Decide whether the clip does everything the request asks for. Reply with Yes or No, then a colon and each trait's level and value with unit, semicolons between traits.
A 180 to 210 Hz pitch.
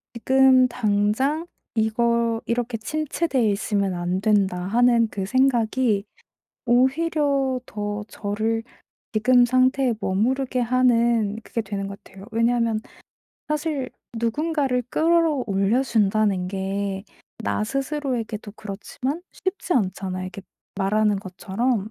No: high, 230 Hz